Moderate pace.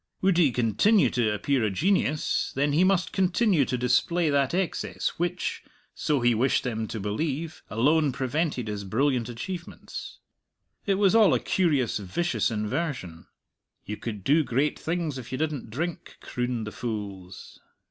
Yes: average, 155 wpm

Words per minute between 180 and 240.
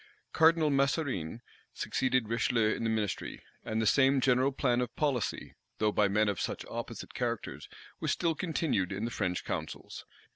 No: average, 160 wpm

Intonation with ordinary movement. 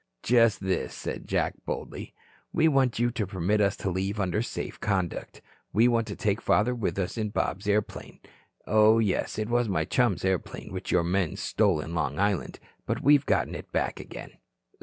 Yes: average, 3.6 semitones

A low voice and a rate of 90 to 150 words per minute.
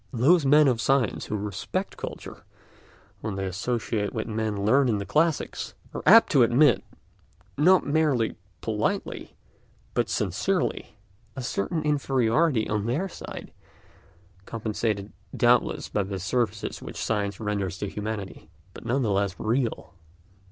Yes: low, 115 Hz; slow, 135 wpm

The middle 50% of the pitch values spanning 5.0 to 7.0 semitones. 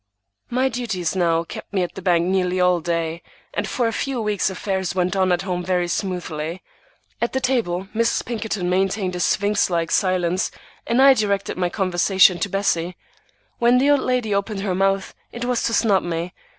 No: average, 3.6 semitones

